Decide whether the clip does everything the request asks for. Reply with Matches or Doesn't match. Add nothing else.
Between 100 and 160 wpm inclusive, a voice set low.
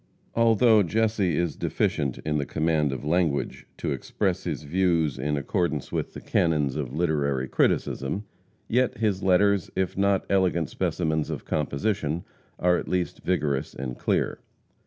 Matches